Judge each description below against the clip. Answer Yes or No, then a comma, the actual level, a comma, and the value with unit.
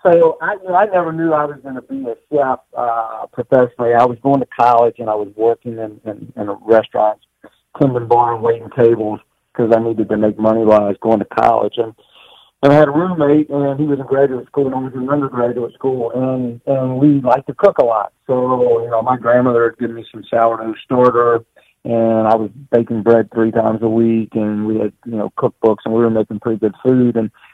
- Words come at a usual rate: No, fast, 230 wpm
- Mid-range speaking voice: No, low, 120 Hz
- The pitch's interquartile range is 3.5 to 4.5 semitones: No, average, 2.8 semitones